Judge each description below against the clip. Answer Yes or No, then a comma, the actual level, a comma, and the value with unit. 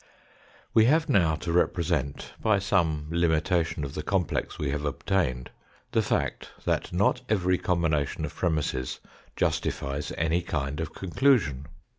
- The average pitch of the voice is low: Yes, very low, 85 Hz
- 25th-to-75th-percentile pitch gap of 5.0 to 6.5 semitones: No, average, 3.9 semitones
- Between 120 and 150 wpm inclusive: Yes, average, 140 wpm